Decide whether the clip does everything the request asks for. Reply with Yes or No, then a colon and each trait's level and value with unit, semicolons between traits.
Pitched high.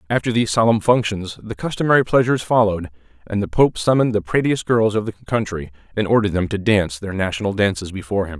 No: low, 105 Hz